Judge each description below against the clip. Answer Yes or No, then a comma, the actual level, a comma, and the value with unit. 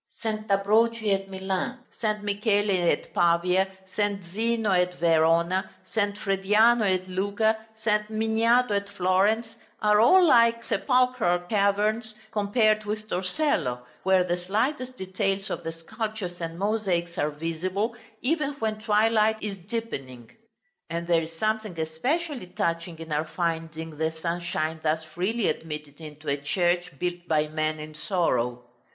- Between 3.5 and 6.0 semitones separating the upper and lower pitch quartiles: Yes, average, 4.5 semitones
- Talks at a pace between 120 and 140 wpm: Yes, slow, 135 wpm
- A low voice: No, high, 195 Hz